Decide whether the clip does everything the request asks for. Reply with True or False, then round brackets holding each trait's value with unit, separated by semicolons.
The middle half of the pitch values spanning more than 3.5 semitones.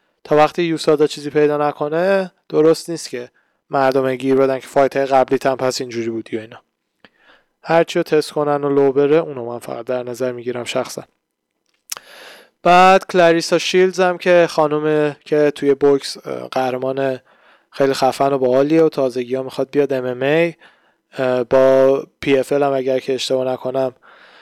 False (3.1 semitones)